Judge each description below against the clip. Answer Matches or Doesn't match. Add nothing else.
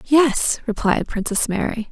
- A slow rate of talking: Matches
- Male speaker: Doesn't match